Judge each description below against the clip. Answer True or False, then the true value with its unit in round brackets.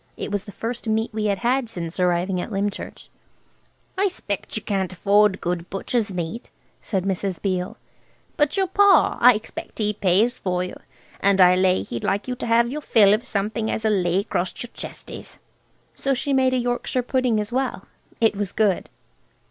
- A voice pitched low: False (210 Hz)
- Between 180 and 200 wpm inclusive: True (185 wpm)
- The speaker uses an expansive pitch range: False (4.3 semitones)